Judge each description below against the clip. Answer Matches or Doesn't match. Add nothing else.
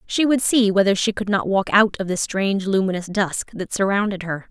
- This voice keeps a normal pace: Doesn't match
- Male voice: Doesn't match